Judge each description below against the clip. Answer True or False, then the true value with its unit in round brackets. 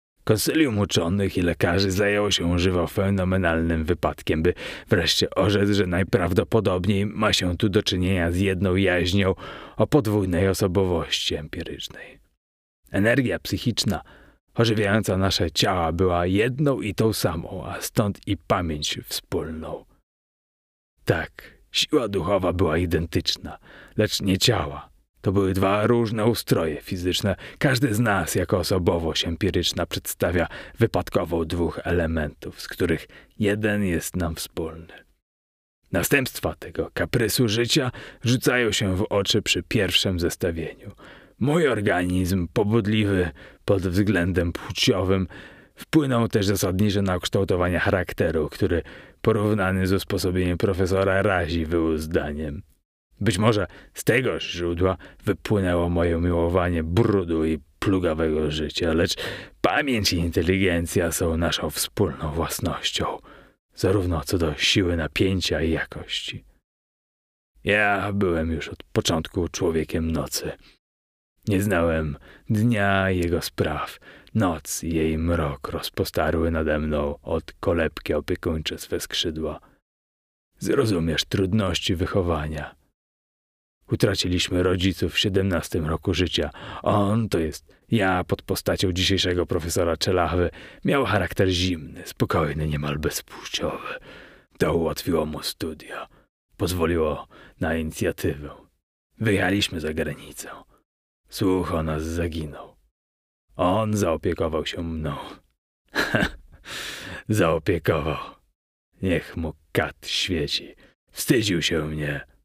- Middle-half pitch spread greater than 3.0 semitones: True (3.6 semitones)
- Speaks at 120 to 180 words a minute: False (110 wpm)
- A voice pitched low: True (90 Hz)